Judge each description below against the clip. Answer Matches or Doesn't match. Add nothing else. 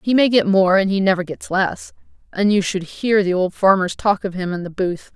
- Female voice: Matches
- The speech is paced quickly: Matches